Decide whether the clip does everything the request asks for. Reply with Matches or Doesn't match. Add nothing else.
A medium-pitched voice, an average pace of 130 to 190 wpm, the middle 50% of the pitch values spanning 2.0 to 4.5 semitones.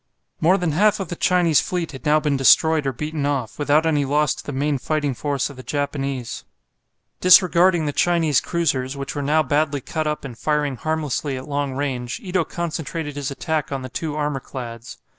Doesn't match